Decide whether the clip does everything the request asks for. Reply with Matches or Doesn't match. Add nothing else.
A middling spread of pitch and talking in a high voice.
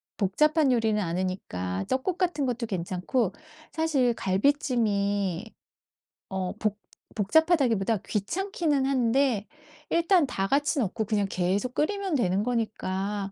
Doesn't match